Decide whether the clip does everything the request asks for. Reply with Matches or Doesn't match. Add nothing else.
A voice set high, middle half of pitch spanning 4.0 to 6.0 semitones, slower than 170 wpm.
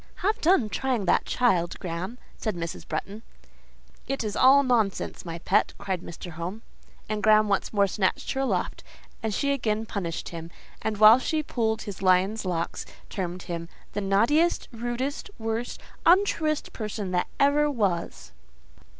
Matches